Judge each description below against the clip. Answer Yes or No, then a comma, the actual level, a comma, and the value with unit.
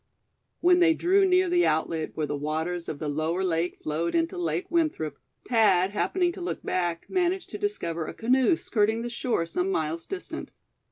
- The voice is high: Yes, high, 205 Hz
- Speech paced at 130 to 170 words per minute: No, average, 180 wpm